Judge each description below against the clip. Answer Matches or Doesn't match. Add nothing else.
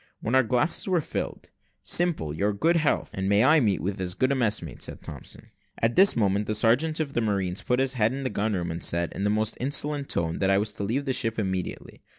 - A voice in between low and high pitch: Doesn't match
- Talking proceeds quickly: Matches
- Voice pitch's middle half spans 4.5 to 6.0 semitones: Matches